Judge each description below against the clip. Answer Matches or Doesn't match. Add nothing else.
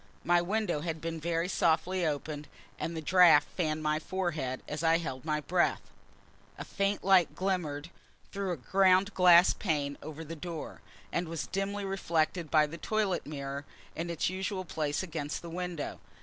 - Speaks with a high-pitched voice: Doesn't match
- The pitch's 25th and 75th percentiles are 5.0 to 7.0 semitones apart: Doesn't match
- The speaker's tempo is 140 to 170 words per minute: Matches